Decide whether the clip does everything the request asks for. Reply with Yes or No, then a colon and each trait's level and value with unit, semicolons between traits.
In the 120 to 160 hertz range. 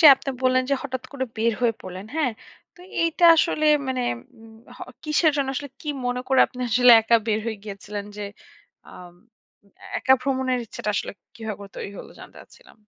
No: very high, 250 Hz